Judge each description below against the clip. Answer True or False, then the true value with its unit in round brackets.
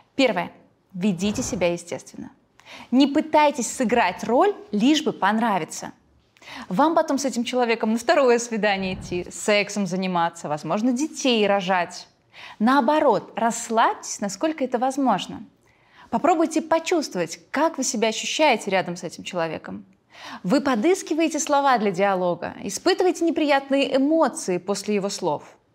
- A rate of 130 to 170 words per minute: False (120 wpm)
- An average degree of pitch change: False (6.4 semitones)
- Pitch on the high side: True (240 Hz)